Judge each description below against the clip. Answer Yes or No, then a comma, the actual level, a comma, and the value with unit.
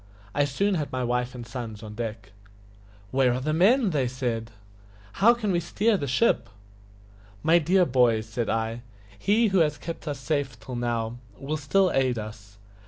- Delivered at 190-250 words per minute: No, average, 175 wpm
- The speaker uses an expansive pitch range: Yes, wide, 6.5 semitones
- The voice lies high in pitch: No, low, 130 Hz